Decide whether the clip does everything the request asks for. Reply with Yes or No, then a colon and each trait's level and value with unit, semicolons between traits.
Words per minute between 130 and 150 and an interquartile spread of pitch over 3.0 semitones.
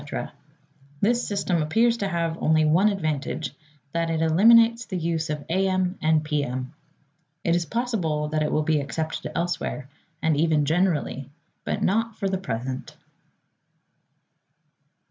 Yes: average, 145 wpm; average, 4.0 semitones